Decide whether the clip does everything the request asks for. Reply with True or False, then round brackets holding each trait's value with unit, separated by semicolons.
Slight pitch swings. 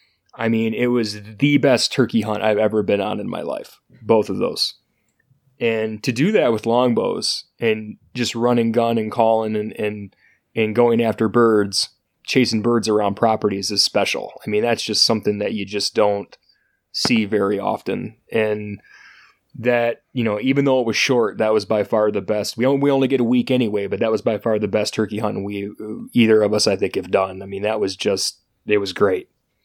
True (2.3 semitones)